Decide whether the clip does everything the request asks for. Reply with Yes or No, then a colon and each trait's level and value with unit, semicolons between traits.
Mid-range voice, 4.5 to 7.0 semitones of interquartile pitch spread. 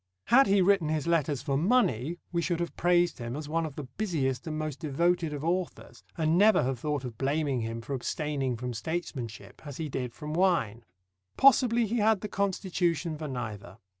Yes: medium, 155 Hz; average, 5.0 semitones